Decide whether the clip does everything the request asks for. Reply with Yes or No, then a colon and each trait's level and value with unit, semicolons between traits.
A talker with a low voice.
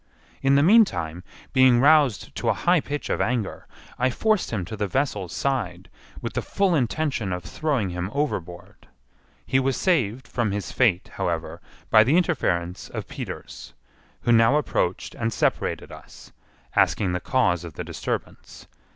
Yes: low, 120 Hz